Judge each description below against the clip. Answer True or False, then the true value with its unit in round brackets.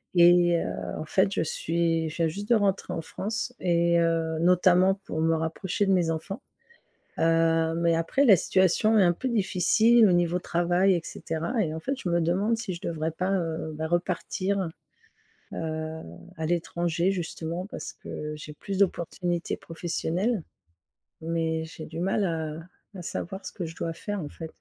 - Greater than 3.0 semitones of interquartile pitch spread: False (2.7 semitones)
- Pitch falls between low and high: True (170 Hz)